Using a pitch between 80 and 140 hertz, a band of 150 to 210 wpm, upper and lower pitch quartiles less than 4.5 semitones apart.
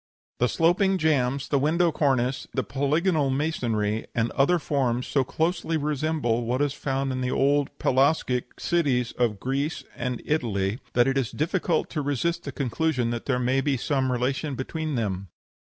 Yes: low, 135 Hz; average, 165 wpm; average, 3.8 semitones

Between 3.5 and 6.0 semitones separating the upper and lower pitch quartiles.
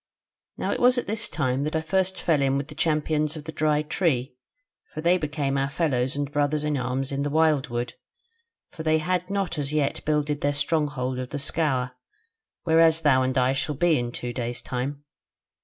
No: average, 3.0 semitones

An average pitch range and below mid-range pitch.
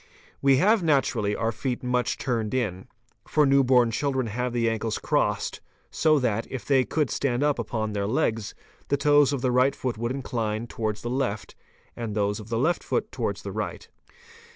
Yes: average, 3.6 semitones; low, 125 Hz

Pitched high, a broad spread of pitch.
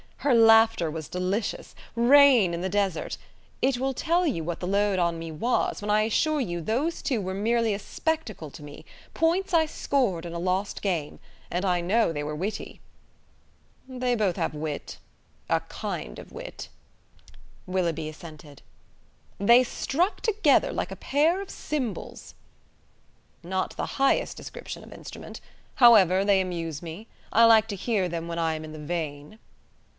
Yes: high, 200 Hz; wide, 6.3 semitones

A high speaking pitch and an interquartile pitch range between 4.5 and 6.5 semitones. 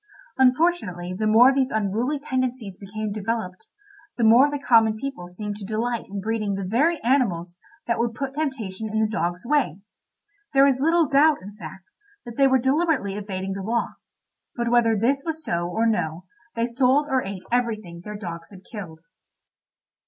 Yes: high, 225 Hz; average, 5.1 semitones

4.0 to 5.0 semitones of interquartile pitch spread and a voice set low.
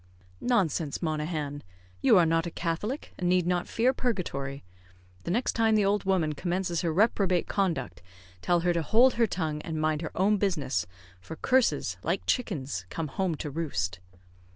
No: average, 4.3 semitones; medium, 170 Hz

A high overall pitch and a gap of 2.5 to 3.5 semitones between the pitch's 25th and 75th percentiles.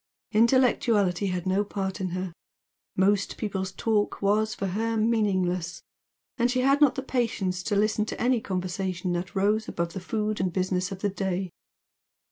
Yes: high, 195 Hz; average, 2.9 semitones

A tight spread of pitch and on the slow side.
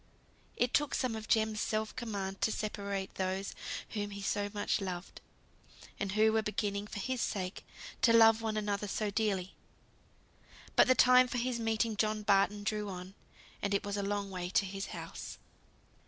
No: narrow, 2.0 semitones; average, 175 wpm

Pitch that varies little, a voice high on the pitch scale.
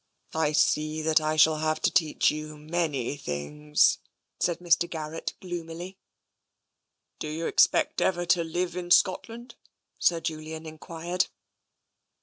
No: narrow, 2.2 semitones; medium, 160 Hz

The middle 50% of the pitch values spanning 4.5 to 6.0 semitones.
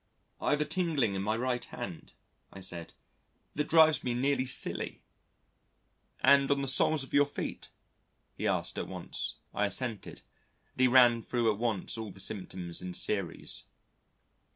Yes: wide, 5.6 semitones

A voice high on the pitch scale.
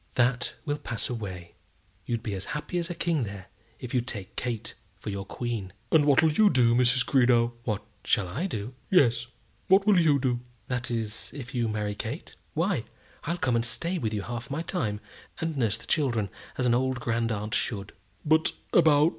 No: low, 120 Hz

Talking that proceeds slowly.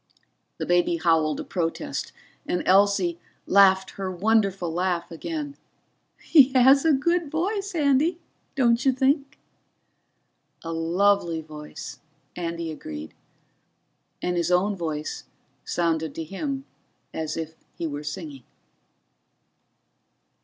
Yes: slow, 110 wpm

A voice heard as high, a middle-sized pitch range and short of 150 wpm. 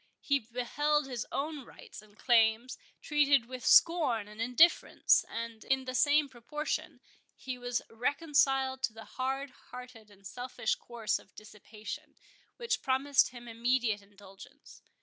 Yes: very high, 250 Hz; average, 3.6 semitones; slow, 135 wpm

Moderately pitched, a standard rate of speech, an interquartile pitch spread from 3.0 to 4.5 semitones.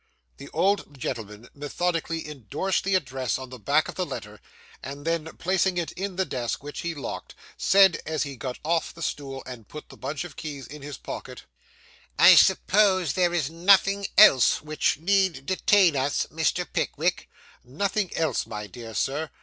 No: medium, 155 Hz; average, 175 wpm; wide, 5.5 semitones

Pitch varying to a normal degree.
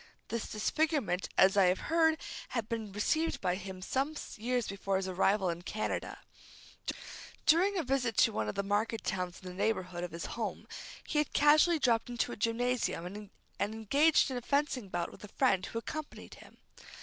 No: wide, 6.2 semitones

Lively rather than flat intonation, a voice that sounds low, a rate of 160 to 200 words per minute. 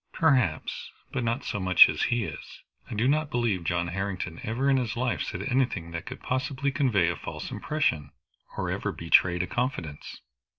Yes: wide, 7.0 semitones; low, 115 Hz; average, 180 wpm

